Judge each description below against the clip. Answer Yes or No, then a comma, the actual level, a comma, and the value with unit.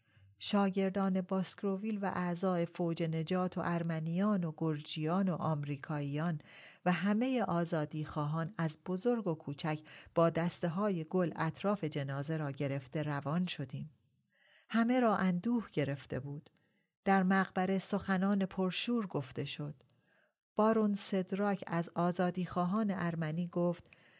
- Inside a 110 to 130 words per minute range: Yes, average, 120 wpm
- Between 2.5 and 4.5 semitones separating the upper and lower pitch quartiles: Yes, average, 3.8 semitones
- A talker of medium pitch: Yes, medium, 175 Hz